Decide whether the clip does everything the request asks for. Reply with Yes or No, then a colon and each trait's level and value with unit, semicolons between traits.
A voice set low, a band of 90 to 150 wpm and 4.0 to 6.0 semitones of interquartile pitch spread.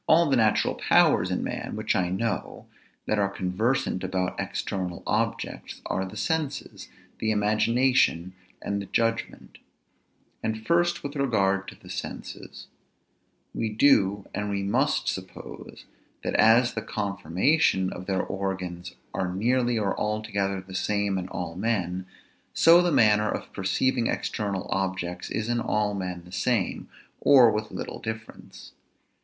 No: low, 105 Hz; average, 140 wpm; average, 3.6 semitones